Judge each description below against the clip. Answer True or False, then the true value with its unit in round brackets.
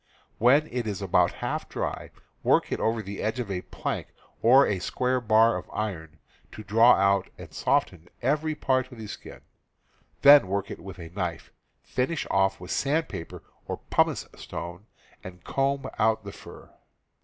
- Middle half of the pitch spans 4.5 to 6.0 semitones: True (5.1 semitones)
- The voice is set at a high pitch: False (110 Hz)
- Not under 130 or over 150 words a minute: False (165 wpm)